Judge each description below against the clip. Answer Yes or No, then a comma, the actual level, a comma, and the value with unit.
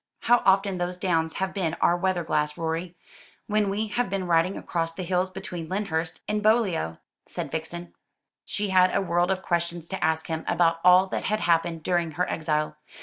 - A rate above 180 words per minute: Yes, average, 190 wpm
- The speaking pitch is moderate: Yes, medium, 175 Hz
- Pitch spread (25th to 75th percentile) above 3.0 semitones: No, narrow, 2.5 semitones